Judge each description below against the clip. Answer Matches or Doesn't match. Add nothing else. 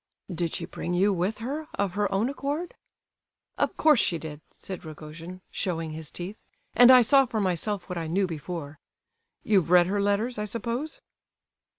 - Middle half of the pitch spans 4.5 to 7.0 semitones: Matches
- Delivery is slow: Doesn't match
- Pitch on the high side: Matches